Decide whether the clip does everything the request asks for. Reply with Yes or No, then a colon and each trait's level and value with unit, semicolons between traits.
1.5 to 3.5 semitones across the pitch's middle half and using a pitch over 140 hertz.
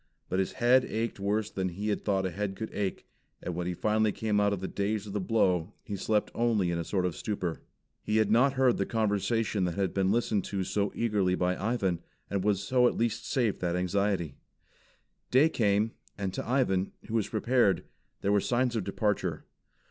No: average, 2.8 semitones; low, 105 Hz